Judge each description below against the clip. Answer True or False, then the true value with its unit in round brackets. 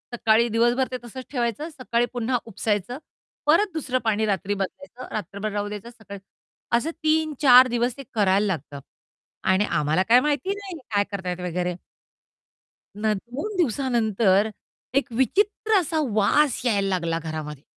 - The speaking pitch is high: True (230 Hz)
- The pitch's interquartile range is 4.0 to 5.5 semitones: True (4.8 semitones)